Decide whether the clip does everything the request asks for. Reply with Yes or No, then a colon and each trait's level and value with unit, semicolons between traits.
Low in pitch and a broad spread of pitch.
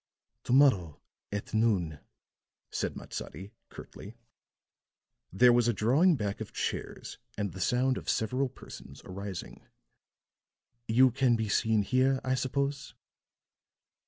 No: low, 115 Hz; average, 4.4 semitones